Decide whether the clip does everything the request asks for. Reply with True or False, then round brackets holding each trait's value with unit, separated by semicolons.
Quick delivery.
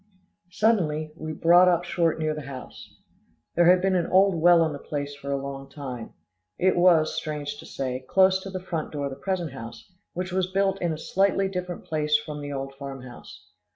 True (210 wpm)